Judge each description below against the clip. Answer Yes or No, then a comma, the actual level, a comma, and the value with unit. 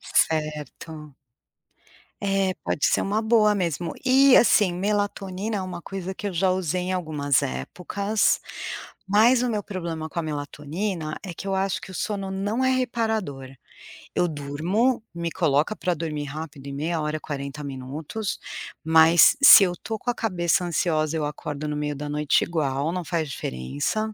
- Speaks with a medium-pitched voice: Yes, medium, 170 Hz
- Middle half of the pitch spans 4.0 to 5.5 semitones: Yes, average, 5.0 semitones